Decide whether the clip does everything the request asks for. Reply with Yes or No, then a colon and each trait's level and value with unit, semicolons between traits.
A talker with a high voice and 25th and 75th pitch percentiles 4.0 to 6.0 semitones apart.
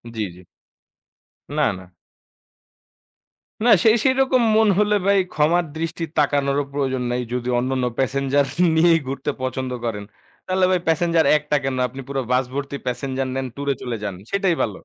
No: medium, 140 Hz; average, 4.4 semitones